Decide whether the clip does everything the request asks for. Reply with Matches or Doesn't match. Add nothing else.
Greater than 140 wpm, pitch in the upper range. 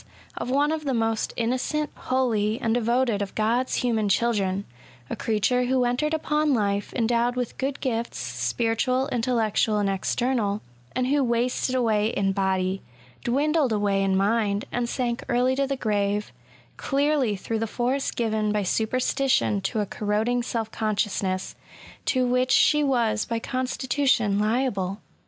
Matches